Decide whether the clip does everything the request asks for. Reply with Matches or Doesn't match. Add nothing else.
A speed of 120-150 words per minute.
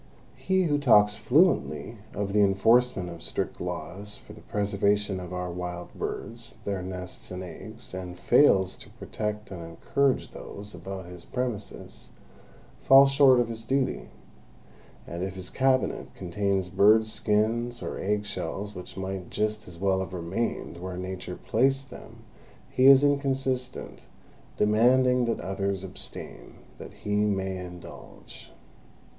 Matches